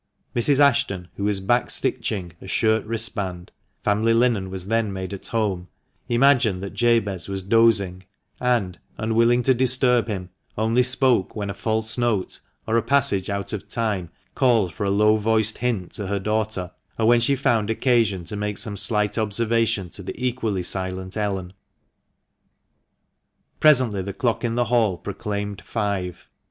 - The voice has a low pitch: Yes, low, 110 Hz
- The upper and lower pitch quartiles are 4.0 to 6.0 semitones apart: No, average, 3.2 semitones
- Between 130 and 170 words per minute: Yes, average, 160 wpm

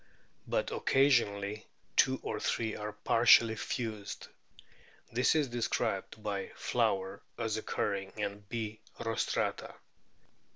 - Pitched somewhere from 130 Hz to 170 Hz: No, low, 110 Hz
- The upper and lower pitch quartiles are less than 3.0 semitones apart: Yes, narrow, 2.4 semitones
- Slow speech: Yes, slow, 100 wpm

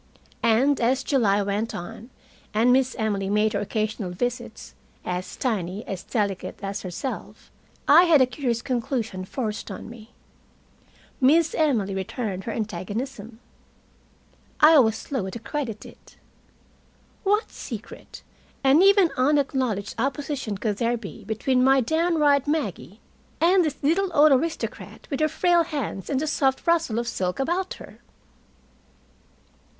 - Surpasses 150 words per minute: No, slow, 135 wpm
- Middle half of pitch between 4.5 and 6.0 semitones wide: Yes, wide, 5.5 semitones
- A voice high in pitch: Yes, high, 245 Hz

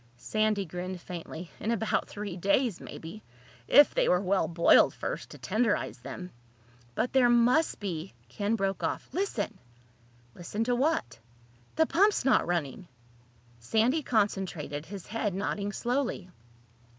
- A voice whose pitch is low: No, high, 200 Hz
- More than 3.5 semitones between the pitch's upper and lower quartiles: Yes, average, 5.3 semitones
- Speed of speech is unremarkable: No, slow, 130 wpm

